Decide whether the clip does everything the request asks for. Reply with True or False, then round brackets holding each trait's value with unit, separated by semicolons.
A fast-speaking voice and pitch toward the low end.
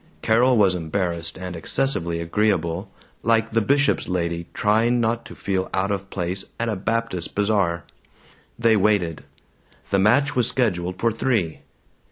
False (145 wpm; 100 Hz)